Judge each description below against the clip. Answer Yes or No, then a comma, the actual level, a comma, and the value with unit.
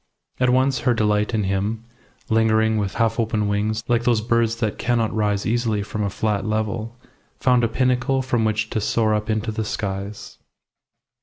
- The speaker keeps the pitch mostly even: Yes, narrow, 1.8 semitones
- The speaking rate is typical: Yes, average, 180 wpm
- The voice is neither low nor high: No, low, 110 Hz